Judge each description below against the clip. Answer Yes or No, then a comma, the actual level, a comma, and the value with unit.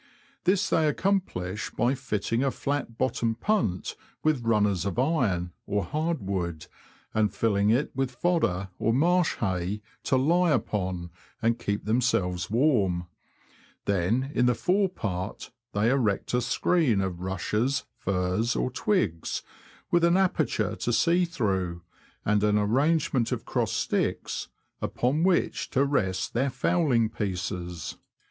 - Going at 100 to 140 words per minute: Yes, slow, 135 wpm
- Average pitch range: No, wide, 7.0 semitones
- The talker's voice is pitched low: Yes, low, 115 Hz